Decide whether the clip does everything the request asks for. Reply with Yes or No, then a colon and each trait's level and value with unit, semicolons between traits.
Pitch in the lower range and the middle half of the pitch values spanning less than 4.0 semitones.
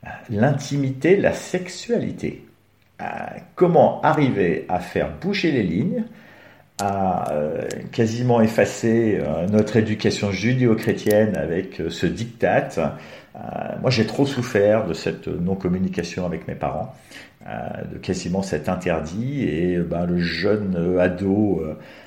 No: low, 105 Hz; average, 5.1 semitones